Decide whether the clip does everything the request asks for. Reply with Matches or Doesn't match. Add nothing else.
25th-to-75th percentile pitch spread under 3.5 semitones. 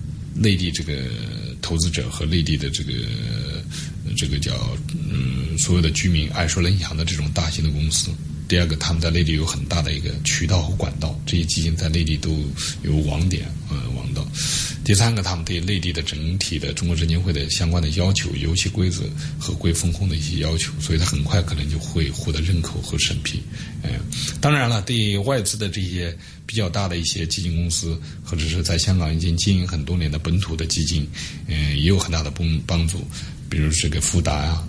Matches